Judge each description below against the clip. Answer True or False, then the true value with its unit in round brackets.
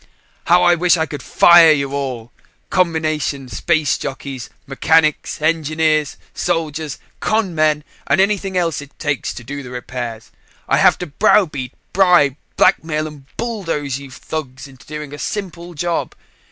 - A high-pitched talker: False (155 Hz)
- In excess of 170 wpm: False (145 wpm)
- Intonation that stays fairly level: False (3.6 semitones)